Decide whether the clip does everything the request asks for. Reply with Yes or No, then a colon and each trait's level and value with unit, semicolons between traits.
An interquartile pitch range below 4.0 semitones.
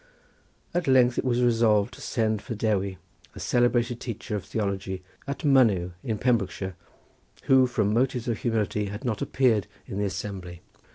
Yes: average, 3.5 semitones